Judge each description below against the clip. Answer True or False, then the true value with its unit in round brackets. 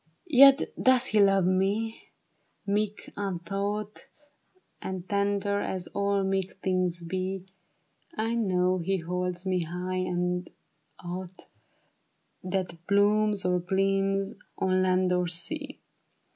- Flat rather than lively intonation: True (1.9 semitones)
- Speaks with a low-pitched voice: False (190 Hz)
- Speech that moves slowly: True (115 wpm)